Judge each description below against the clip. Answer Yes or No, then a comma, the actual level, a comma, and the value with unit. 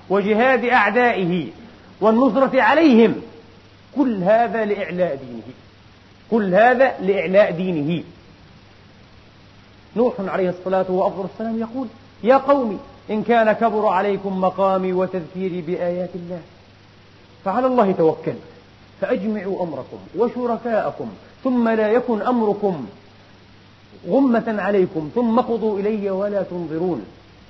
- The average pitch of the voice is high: Yes, high, 195 Hz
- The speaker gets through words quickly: No, average, 95 wpm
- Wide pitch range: Yes, wide, 6.1 semitones